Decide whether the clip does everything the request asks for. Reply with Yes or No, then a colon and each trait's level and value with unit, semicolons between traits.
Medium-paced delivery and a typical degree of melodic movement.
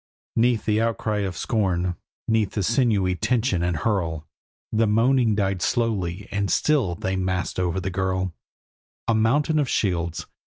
Yes: average, 150 wpm; average, 3.8 semitones